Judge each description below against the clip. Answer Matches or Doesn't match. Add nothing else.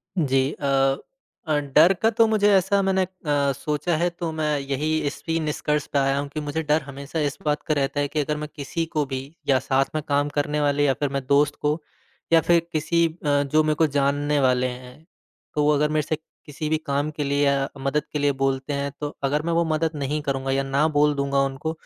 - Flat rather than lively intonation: Matches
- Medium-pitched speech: Matches